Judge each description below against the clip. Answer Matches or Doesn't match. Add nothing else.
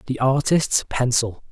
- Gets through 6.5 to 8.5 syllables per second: Doesn't match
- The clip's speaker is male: Matches